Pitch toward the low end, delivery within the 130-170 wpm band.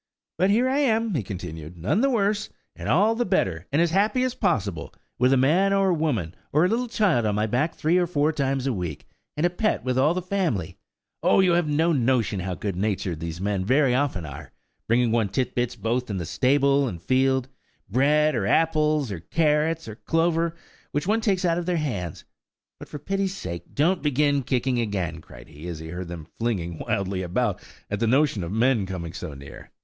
No: low, 130 Hz; fast, 205 wpm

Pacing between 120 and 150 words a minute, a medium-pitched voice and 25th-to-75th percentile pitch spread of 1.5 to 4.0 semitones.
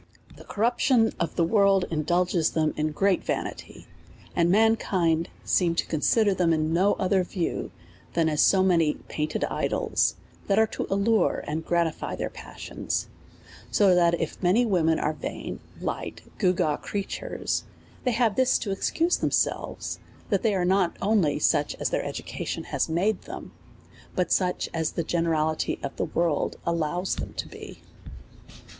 No: average, 160 wpm; medium, 180 Hz; average, 3.6 semitones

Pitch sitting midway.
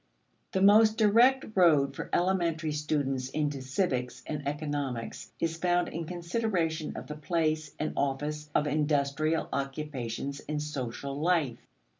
Yes: medium, 150 Hz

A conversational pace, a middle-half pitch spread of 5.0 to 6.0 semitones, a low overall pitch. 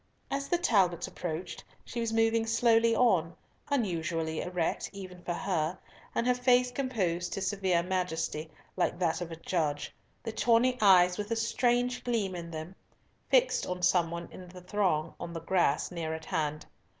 No: average, 170 wpm; average, 5.3 semitones; medium, 185 Hz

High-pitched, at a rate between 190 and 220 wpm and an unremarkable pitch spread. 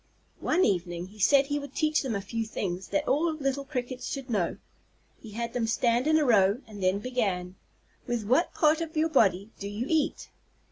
No: high, 240 Hz; average, 200 wpm; wide, 6.0 semitones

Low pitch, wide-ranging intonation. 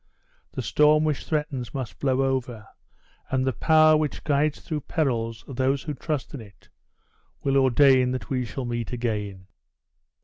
No: low, 130 Hz; average, 3.6 semitones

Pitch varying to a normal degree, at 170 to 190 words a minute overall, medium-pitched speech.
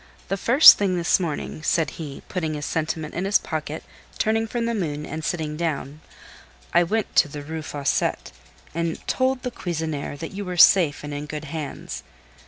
Yes: average, 4.0 semitones; average, 185 wpm; medium, 160 Hz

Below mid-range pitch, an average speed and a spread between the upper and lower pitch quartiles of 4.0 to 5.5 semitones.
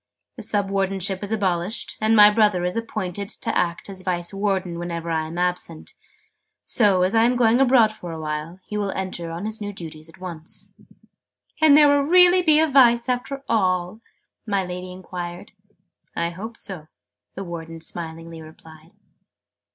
No: high, 190 Hz; average, 170 wpm; average, 4.4 semitones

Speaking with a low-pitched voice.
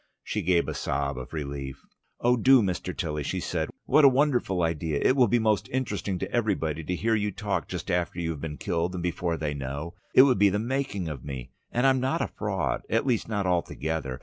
Yes: very low, 90 Hz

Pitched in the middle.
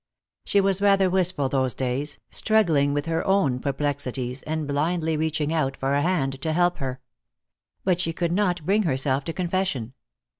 Yes: medium, 155 Hz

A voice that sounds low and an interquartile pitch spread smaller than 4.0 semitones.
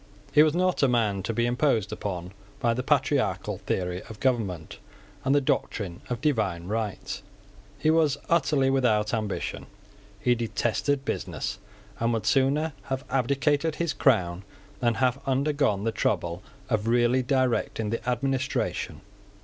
No: low, 120 Hz; average, 4.6 semitones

